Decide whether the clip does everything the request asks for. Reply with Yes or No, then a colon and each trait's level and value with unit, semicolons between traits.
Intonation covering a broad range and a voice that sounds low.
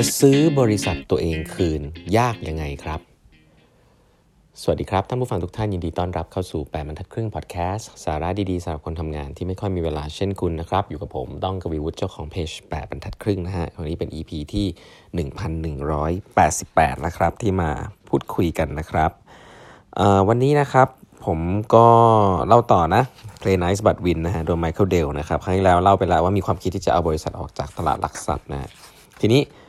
No: average, 3.7 semitones; very low, 90 Hz